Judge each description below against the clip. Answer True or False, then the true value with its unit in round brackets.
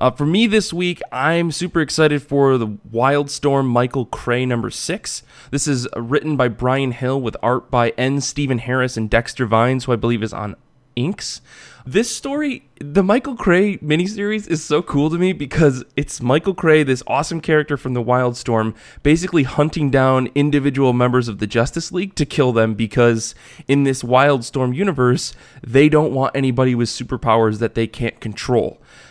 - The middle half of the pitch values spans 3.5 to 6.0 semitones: True (3.9 semitones)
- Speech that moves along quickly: False (175 wpm)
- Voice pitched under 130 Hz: False (135 Hz)